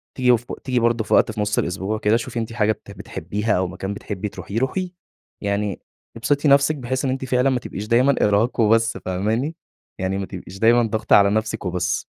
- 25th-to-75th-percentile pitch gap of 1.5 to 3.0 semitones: No, average, 3.7 semitones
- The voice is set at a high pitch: No, low, 110 Hz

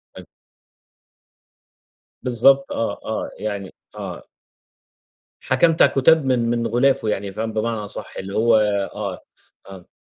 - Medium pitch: No, low, 115 Hz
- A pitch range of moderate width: Yes, average, 4.0 semitones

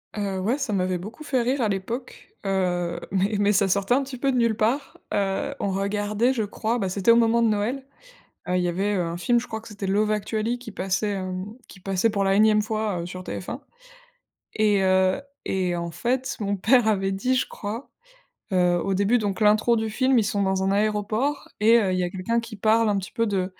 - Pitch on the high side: Yes, high, 210 Hz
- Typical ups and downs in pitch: Yes, average, 3.2 semitones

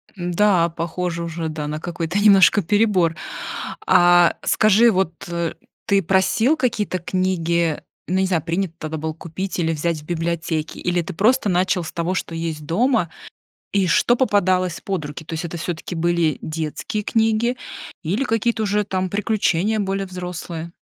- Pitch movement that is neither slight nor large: Yes, average, 3.3 semitones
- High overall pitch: No, medium, 180 Hz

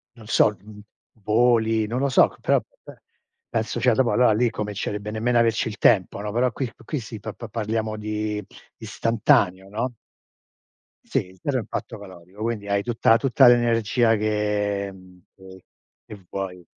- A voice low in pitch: Yes, low, 110 Hz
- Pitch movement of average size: No, narrow, 2.3 semitones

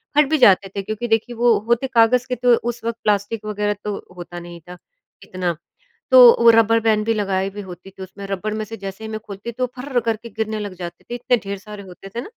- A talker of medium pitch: No, high, 215 Hz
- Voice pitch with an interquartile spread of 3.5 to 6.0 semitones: No, average, 3.0 semitones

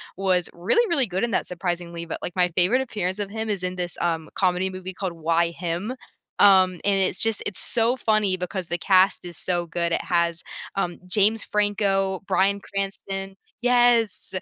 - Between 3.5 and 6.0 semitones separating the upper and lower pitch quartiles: No, average, 2.7 semitones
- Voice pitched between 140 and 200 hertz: Yes, high, 190 Hz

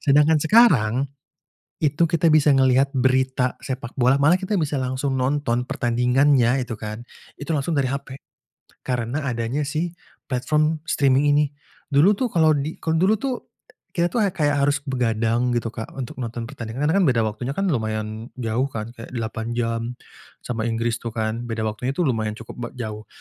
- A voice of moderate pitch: No, low, 130 Hz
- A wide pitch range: No, average, 4.0 semitones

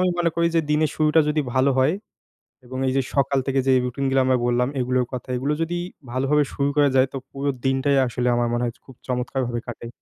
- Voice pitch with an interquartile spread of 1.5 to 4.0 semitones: Yes, narrow, 2.6 semitones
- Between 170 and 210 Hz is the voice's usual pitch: No, low, 135 Hz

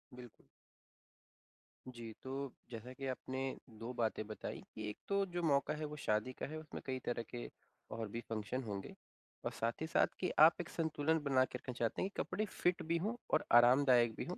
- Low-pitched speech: Yes, low, 130 Hz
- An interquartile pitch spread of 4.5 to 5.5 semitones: Yes, average, 5.2 semitones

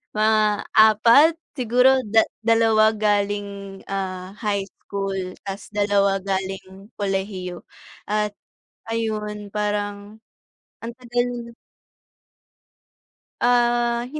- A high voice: Yes, high, 210 Hz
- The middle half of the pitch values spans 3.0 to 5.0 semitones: No, narrow, 2.4 semitones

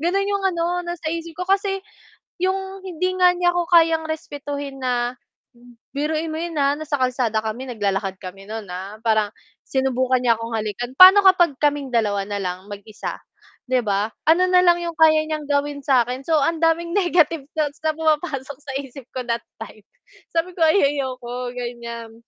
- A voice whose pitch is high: Yes, very high, 285 Hz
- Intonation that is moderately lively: No, wide, 5.8 semitones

